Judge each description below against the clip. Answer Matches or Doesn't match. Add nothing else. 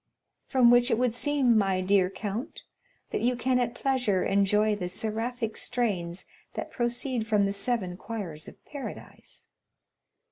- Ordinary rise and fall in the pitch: Matches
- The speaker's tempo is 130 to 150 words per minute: Matches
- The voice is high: Matches